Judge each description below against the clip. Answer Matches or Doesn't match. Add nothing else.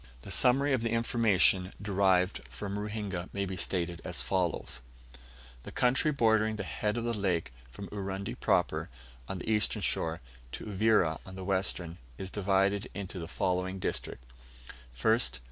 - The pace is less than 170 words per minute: Matches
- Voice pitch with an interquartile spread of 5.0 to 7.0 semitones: Doesn't match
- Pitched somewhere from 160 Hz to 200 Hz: Doesn't match